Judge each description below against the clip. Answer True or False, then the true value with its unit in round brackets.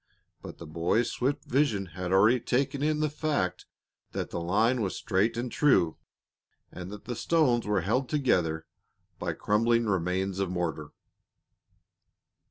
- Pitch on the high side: False (105 Hz)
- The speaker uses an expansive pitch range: True (5.8 semitones)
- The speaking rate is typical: True (145 wpm)